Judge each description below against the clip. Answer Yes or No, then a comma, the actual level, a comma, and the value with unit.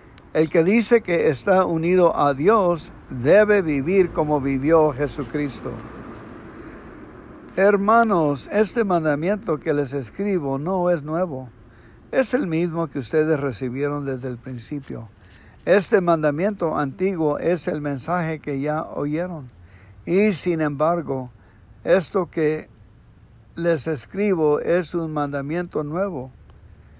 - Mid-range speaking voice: Yes, medium, 155 Hz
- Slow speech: Yes, slow, 115 wpm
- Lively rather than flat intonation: No, average, 4.9 semitones